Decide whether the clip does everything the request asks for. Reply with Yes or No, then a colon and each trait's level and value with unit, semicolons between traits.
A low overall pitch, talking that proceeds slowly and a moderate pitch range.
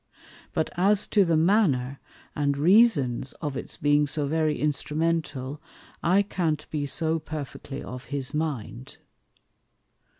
No: medium, 150 Hz; slow, 125 wpm; average, 3.1 semitones